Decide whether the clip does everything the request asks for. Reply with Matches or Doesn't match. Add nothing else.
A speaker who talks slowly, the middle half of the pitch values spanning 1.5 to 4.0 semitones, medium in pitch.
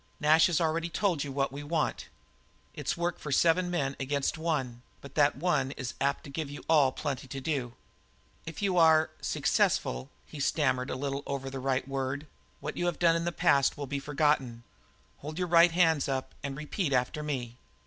Doesn't match